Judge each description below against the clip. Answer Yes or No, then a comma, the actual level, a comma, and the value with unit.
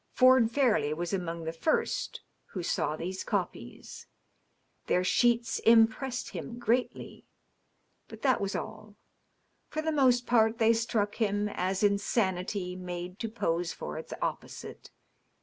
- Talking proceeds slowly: Yes, slow, 130 wpm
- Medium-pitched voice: No, high, 215 Hz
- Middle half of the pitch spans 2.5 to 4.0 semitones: No, average, 4.7 semitones